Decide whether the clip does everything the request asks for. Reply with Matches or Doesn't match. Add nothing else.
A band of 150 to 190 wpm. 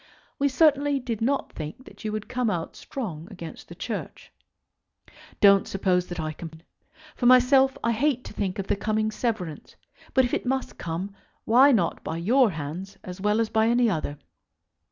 Matches